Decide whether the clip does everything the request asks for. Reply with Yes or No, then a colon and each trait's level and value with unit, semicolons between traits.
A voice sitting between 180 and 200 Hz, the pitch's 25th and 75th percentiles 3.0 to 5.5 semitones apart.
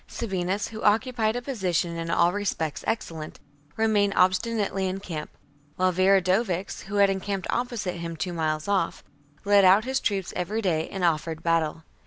Yes: high, 190 Hz; average, 3.3 semitones